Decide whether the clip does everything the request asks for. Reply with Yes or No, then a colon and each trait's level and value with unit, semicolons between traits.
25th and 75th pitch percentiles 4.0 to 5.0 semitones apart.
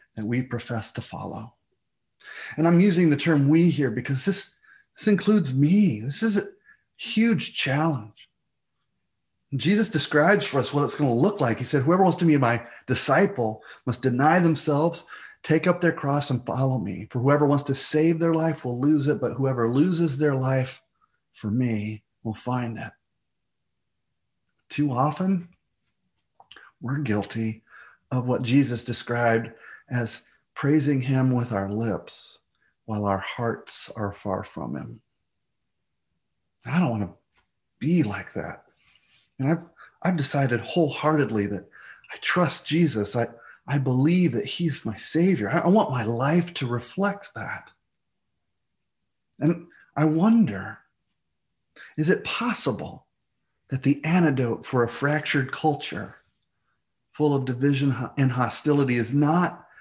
No: wide, 5.4 semitones